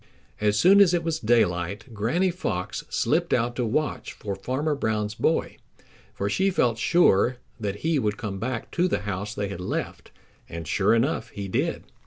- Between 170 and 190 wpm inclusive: Yes, average, 180 wpm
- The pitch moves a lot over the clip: Yes, wide, 7.2 semitones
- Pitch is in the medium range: No, low, 110 Hz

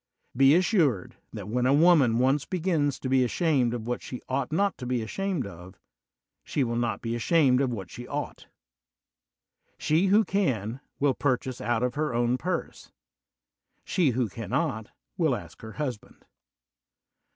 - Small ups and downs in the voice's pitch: No, average, 4.7 semitones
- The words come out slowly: No, average, 160 wpm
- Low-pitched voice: Yes, low, 130 Hz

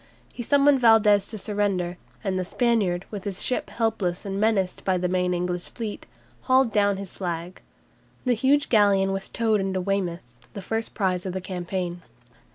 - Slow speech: No, average, 170 wpm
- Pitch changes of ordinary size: Yes, average, 3.5 semitones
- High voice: Yes, high, 195 Hz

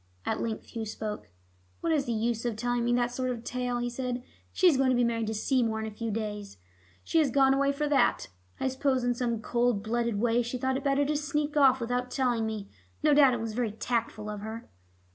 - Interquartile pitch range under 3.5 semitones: Yes, average, 2.8 semitones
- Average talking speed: No, fast, 240 wpm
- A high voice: Yes, high, 245 Hz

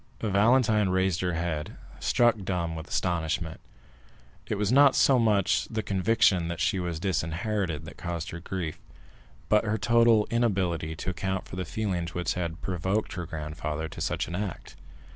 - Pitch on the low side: Yes, very low, 90 Hz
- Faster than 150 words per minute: Yes, average, 160 wpm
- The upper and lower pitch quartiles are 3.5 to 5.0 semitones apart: Yes, average, 4.0 semitones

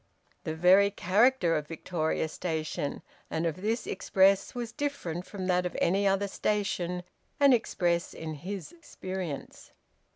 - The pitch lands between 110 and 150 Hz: No, medium, 185 Hz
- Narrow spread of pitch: No, average, 3.3 semitones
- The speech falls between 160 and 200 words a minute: No, slow, 135 wpm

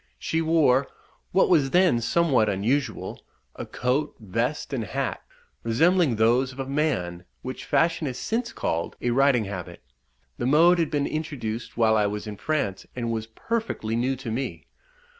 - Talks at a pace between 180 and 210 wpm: No, average, 160 wpm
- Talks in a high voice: No, low, 130 Hz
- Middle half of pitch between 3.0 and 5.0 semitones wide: No, wide, 5.5 semitones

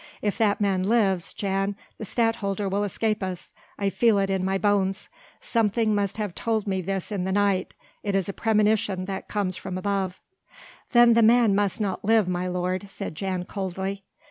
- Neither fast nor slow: Yes, average, 185 wpm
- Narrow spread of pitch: Yes, narrow, 1.9 semitones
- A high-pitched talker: Yes, high, 200 Hz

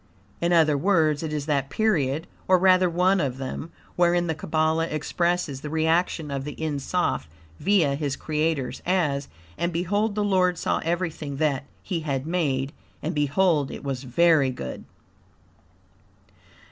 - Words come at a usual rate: Yes, average, 150 wpm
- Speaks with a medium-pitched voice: Yes, medium, 160 Hz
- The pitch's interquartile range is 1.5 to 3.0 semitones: No, average, 3.8 semitones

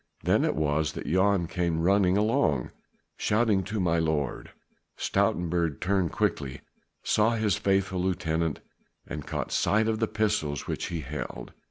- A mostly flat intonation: No, average, 4.5 semitones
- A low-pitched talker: Yes, very low, 90 Hz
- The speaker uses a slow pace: No, average, 145 wpm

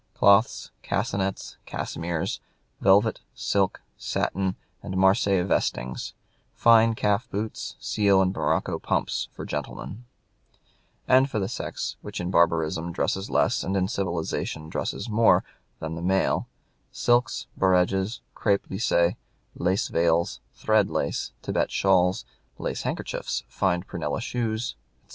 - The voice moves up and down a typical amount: Yes, average, 3.3 semitones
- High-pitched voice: No, very low, 95 Hz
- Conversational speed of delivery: No, slow, 120 wpm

